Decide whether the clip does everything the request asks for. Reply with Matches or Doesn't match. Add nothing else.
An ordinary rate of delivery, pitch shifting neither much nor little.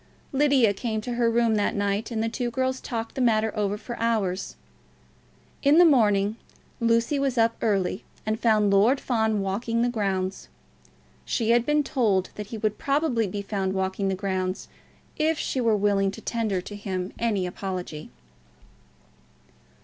Matches